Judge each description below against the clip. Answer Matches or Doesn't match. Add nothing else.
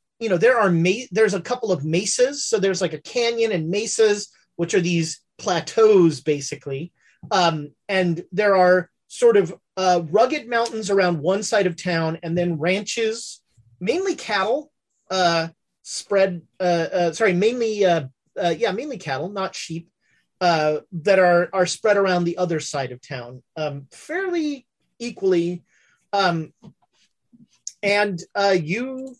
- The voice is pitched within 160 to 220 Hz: Matches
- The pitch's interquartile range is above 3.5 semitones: Matches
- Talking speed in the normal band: Matches